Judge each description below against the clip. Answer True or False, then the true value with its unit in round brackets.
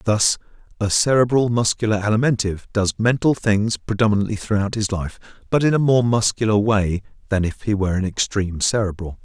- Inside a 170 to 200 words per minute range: False (160 wpm)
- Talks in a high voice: False (105 Hz)